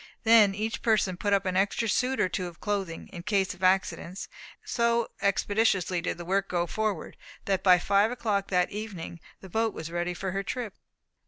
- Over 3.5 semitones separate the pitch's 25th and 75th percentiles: No, average, 3.0 semitones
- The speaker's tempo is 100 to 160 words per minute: No, average, 195 wpm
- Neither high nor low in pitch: No, high, 195 Hz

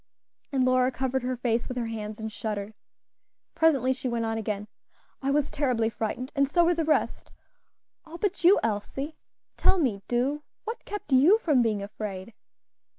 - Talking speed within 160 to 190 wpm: Yes, average, 170 wpm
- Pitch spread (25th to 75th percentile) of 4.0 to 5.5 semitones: Yes, average, 4.9 semitones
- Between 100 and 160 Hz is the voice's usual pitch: No, very high, 255 Hz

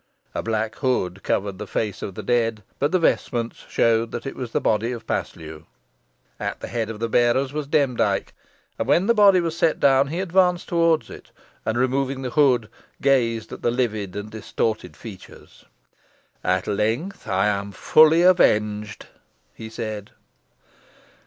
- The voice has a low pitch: Yes, low, 115 Hz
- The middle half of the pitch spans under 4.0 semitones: No, average, 4.8 semitones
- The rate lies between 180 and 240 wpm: No, average, 165 wpm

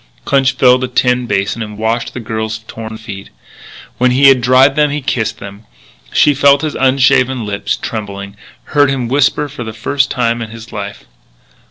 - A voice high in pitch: No, low, 120 Hz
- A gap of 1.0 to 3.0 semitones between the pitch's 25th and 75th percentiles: No, average, 3.5 semitones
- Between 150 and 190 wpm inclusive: Yes, average, 180 wpm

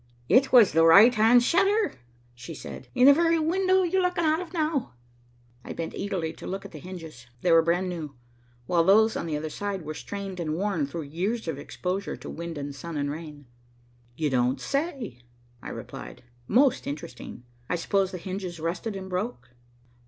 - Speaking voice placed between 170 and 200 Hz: Yes, medium, 185 Hz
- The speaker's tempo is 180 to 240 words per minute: Yes, average, 190 wpm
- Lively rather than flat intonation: Yes, wide, 7.5 semitones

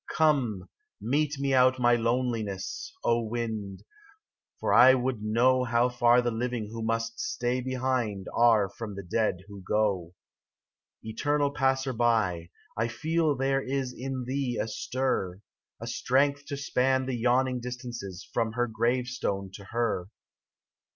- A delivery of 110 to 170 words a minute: Yes, average, 145 wpm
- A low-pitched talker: Yes, low, 120 Hz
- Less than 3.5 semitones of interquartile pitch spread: Yes, average, 2.9 semitones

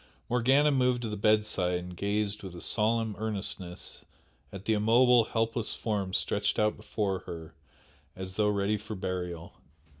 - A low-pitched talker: Yes, low, 105 Hz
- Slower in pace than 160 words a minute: Yes, average, 150 wpm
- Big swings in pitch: No, average, 3.1 semitones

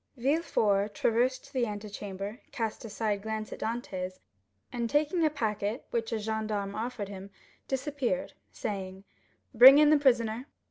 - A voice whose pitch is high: Yes, high, 225 Hz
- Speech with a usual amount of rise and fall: Yes, average, 3.9 semitones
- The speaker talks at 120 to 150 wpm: Yes, average, 140 wpm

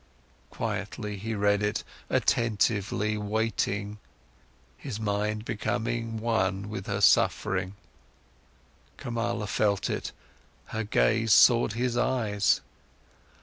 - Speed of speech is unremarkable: No, slow, 95 wpm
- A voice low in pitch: Yes, low, 105 Hz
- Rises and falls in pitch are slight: Yes, narrow, 1.9 semitones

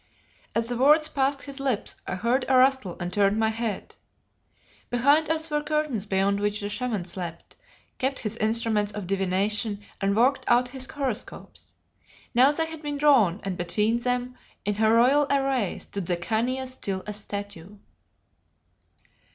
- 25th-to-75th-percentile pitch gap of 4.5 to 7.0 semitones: Yes, average, 4.8 semitones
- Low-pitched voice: No, high, 230 Hz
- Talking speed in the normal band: Yes, average, 160 wpm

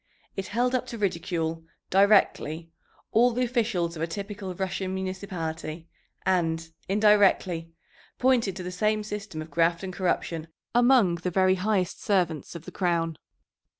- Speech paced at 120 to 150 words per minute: Yes, average, 145 wpm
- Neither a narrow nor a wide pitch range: Yes, average, 3.8 semitones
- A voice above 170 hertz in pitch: Yes, medium, 185 Hz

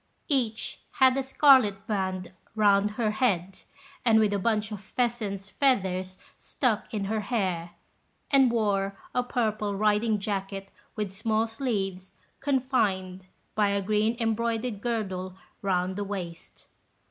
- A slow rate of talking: Yes, slow, 125 wpm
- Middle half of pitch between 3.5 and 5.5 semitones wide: No, average, 3.0 semitones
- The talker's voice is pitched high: Yes, high, 210 Hz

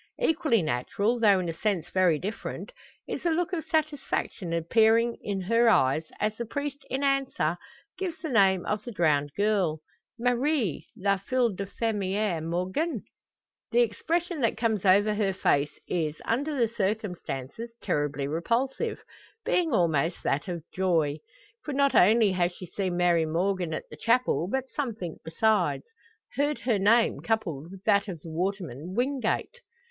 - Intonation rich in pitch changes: Yes, wide, 5.8 semitones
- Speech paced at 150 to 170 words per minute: Yes, average, 155 wpm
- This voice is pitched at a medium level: No, high, 205 Hz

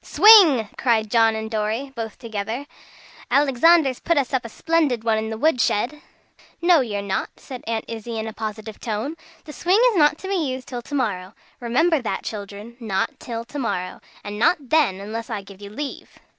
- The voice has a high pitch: Yes, high, 235 Hz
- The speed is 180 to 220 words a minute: Yes, average, 195 wpm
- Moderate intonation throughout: Yes, average, 4.9 semitones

